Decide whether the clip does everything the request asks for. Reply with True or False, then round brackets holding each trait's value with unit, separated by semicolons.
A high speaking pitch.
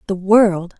True (195 Hz)